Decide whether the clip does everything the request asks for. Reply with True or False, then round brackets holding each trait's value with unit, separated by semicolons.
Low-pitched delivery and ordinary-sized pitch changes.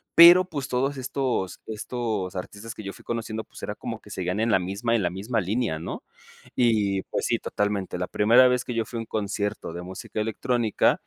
True (110 Hz; 3.9 semitones)